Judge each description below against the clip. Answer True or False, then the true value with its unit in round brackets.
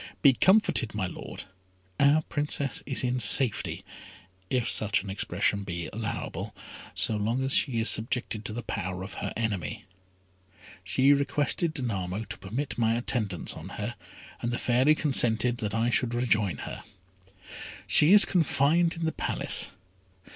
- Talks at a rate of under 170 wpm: True (150 wpm)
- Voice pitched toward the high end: False (120 Hz)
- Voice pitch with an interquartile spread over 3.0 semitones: True (4.9 semitones)